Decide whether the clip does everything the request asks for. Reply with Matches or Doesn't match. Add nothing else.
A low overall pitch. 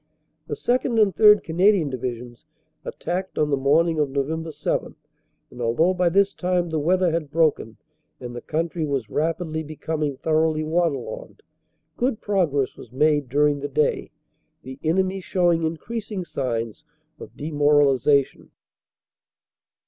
Doesn't match